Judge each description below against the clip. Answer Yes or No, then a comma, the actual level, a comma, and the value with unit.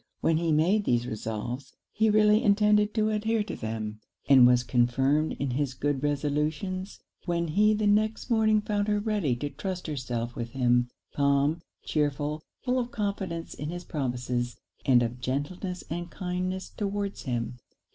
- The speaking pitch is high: No, medium, 155 Hz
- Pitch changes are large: Yes, wide, 8.1 semitones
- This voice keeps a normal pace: Yes, average, 155 wpm